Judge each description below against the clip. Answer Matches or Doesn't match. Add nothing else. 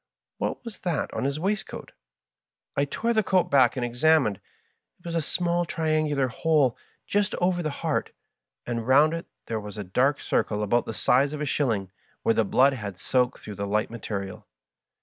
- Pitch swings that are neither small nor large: Doesn't match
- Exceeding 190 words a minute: Doesn't match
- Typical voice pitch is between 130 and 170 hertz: Matches